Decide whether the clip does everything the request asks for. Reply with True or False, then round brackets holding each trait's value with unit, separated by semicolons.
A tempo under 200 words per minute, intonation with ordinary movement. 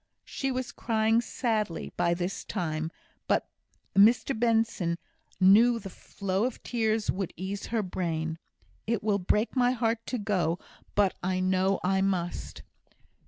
True (140 wpm; 3.7 semitones)